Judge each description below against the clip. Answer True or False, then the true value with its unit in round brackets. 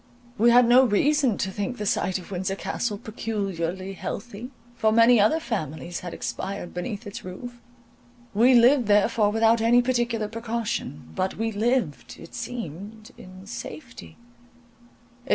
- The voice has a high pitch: True (220 Hz)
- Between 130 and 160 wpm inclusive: True (140 wpm)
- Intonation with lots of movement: False (3.7 semitones)